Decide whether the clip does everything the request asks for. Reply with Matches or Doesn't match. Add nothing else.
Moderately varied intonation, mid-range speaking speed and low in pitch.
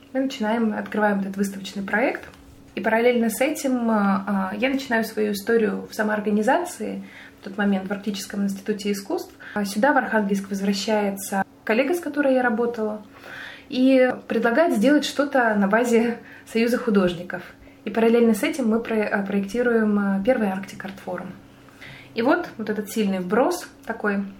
Doesn't match